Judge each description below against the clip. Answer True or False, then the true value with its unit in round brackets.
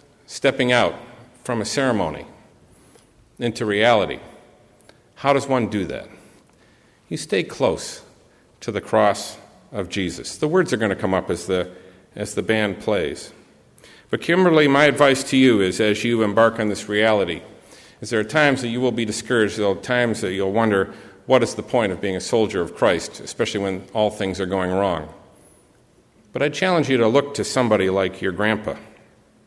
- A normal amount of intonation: True (3.9 semitones)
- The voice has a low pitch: True (110 Hz)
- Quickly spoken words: False (180 wpm)